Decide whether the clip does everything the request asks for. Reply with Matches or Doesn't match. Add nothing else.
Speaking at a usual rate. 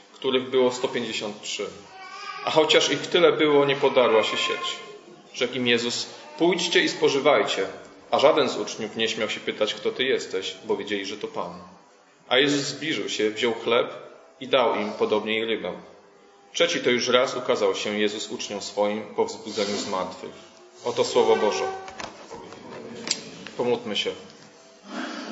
Matches